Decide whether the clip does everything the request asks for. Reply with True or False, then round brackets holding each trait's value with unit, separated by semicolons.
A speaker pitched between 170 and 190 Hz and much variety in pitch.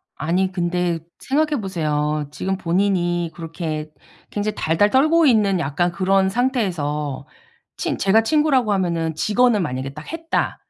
False (185 Hz; 4.9 semitones)